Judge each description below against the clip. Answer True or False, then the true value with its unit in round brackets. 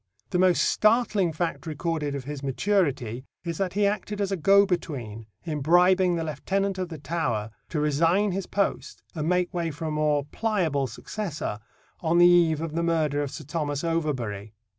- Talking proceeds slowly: False (185 wpm)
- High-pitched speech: False (165 Hz)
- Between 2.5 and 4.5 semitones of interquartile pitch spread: True (4.0 semitones)